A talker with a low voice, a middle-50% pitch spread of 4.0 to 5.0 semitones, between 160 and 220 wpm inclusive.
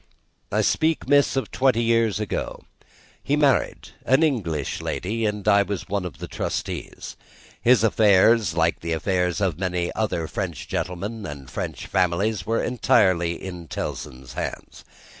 No: low, 100 Hz; average, 4.7 semitones; average, 145 wpm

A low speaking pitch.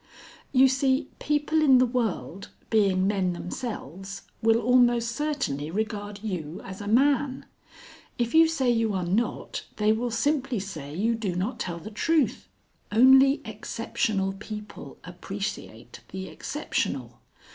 No: high, 220 Hz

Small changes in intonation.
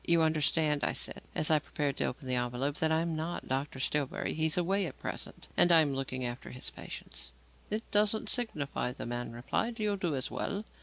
No: average, 4.7 semitones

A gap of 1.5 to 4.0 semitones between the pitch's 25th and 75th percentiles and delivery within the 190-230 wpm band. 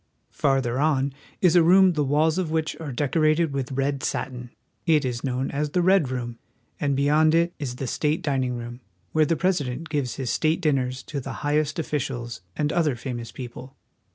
Yes: average, 3.5 semitones; average, 200 wpm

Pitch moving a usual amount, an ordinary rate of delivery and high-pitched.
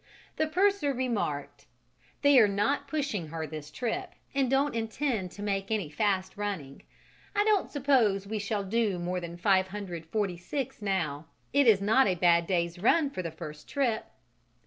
No: wide, 7.2 semitones; average, 160 wpm; high, 205 Hz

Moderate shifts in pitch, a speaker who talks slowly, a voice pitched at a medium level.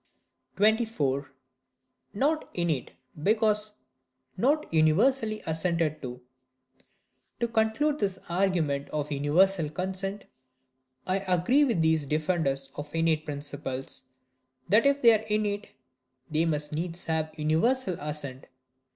No: wide, 6.2 semitones; slow, 105 wpm; medium, 165 Hz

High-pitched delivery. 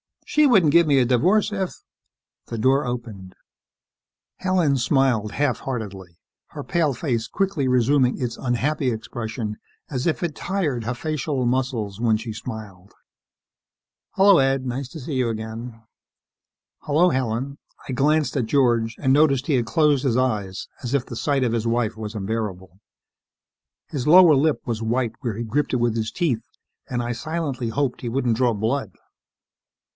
No: low, 125 Hz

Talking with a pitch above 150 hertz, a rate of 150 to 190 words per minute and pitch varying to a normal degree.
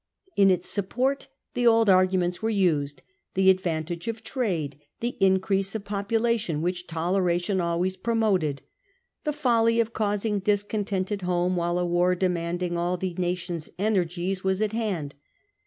Yes: medium, 185 Hz; average, 170 wpm; average, 3.3 semitones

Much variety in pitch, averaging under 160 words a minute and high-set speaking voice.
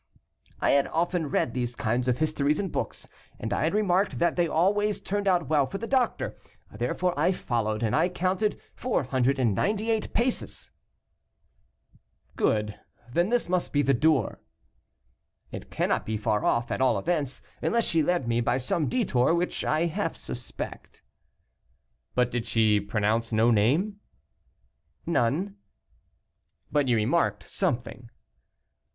No: wide, 7.4 semitones; average, 140 wpm; medium, 150 Hz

